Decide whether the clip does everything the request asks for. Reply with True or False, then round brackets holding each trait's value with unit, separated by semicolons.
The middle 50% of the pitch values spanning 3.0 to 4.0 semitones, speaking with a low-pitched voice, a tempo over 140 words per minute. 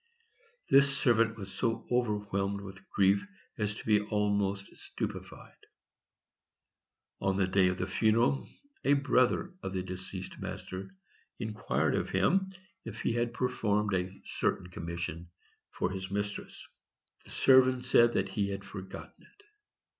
False (3.6 semitones; 100 Hz; 135 wpm)